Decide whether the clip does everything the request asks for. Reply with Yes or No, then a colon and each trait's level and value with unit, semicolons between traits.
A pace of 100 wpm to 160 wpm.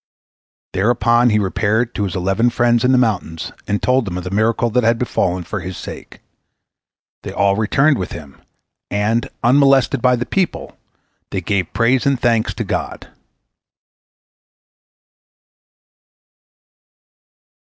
Yes: slow, 135 wpm